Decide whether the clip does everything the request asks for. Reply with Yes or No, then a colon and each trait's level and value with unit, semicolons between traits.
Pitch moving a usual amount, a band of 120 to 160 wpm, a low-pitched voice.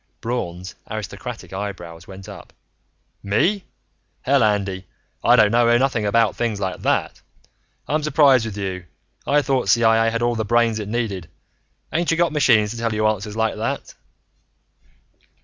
Yes: average, 3.1 semitones; average, 150 wpm; low, 110 Hz